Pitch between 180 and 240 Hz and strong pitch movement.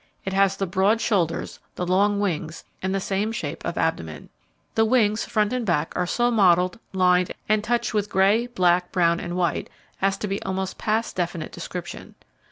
No: high, 190 Hz; average, 3.1 semitones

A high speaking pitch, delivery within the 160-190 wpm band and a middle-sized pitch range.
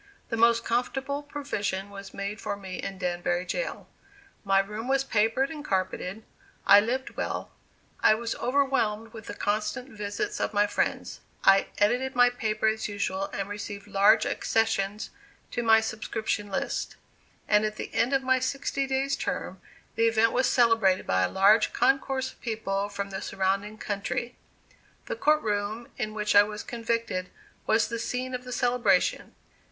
Yes: high, 220 Hz; average, 165 wpm; average, 3.5 semitones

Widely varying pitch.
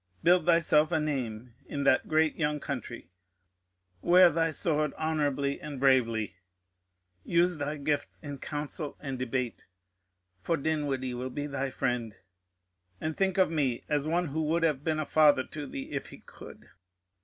No: average, 3.2 semitones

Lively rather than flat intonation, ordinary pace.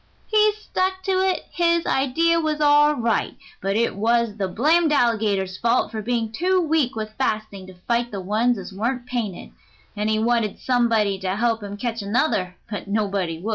Yes: wide, 6.2 semitones; average, 180 wpm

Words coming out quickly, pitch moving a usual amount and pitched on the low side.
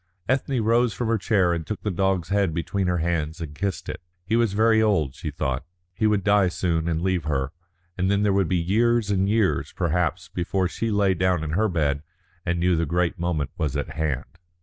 Yes: fast, 215 wpm; average, 3.8 semitones; very low, 90 Hz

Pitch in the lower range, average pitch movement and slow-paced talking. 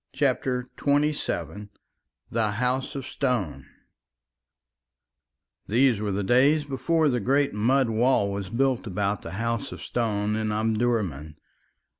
Yes: low, 115 Hz; average, 4.3 semitones; slow, 120 wpm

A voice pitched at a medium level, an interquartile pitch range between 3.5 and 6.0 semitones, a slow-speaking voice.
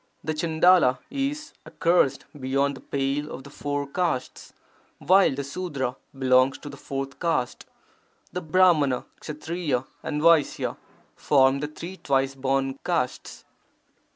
Yes: medium, 145 Hz; average, 3.8 semitones; slow, 125 wpm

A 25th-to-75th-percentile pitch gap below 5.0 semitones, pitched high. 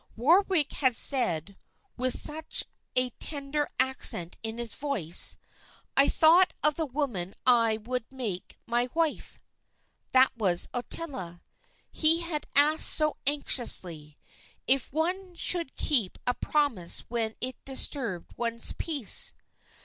No: average, 5.3 semitones; very high, 260 Hz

